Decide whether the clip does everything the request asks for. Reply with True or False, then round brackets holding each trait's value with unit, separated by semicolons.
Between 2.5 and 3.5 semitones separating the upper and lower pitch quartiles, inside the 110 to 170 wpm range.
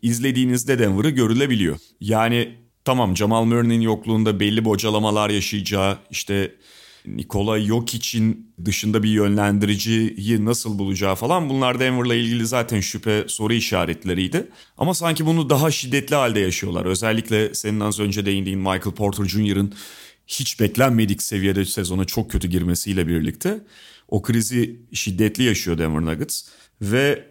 True (2.9 semitones; 125 wpm)